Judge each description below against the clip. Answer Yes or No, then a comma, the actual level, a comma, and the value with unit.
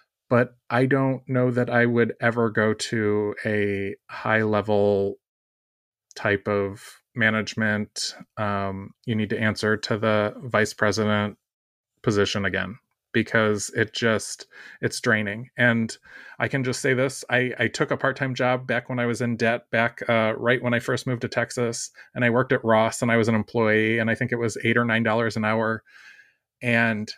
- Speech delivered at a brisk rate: No, average, 180 wpm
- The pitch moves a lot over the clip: No, narrow, 2.4 semitones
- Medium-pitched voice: No, low, 115 Hz